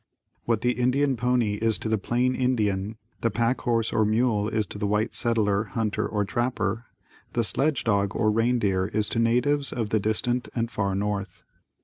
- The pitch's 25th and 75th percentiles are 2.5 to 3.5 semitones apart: Yes, average, 2.8 semitones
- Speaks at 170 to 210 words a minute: Yes, average, 180 wpm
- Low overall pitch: Yes, low, 115 Hz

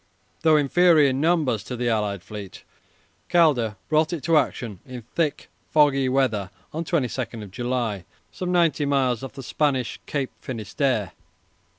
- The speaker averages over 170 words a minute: No, average, 145 wpm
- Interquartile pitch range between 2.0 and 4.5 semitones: No, average, 5.0 semitones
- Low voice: Yes, low, 130 Hz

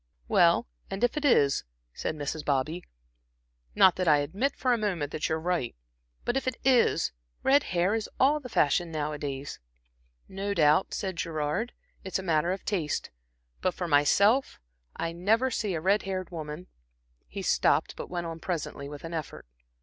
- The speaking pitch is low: No, medium, 175 Hz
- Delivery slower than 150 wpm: No, average, 175 wpm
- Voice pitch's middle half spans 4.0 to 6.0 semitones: Yes, average, 5.1 semitones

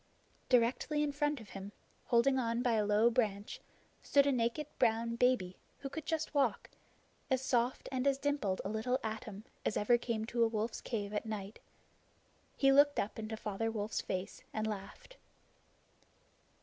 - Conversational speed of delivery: Yes, average, 165 wpm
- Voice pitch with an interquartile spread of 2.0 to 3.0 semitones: No, average, 3.7 semitones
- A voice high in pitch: Yes, high, 230 Hz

